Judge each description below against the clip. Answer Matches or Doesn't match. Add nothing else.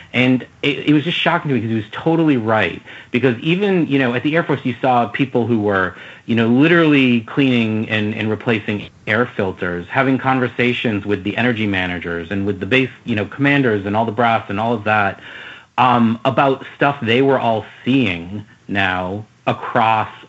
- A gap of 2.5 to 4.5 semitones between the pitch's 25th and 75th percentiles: Matches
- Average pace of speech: Matches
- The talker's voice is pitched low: Matches